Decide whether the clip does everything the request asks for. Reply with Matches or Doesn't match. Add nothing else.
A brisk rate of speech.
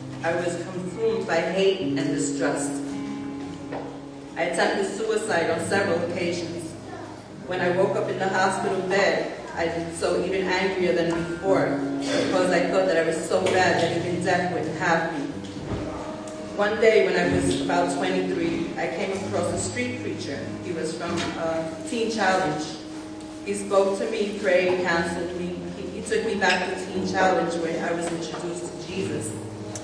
Doesn't match